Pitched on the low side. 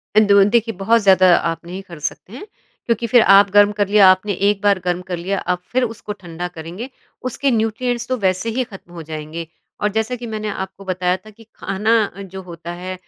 No: high, 200 Hz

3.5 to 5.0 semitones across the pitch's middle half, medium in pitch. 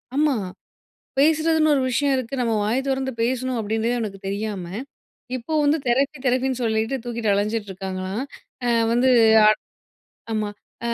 No: average, 3.8 semitones; high, 235 Hz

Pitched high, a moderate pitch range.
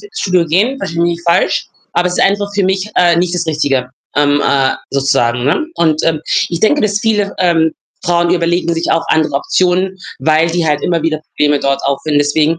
No: medium, 165 Hz; average, 3.5 semitones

